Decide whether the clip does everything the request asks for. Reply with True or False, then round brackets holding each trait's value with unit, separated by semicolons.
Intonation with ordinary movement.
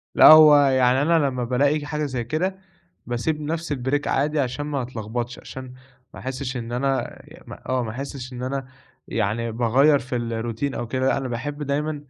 True (3.1 semitones)